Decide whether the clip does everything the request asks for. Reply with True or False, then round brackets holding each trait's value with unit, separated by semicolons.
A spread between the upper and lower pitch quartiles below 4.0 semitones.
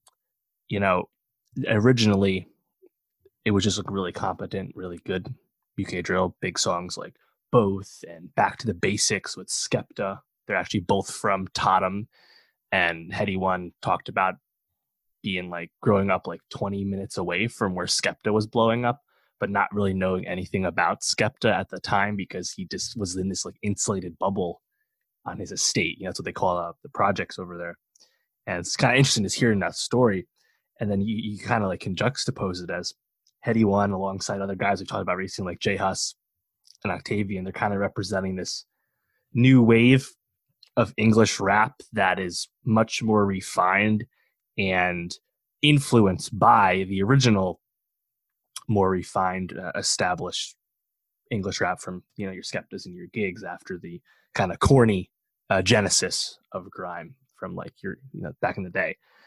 True (3.3 semitones)